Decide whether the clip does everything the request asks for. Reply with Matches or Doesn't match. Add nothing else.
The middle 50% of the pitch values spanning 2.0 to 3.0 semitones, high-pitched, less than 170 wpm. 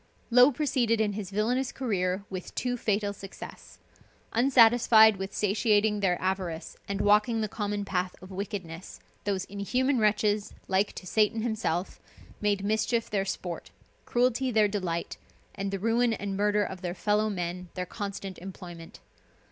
Matches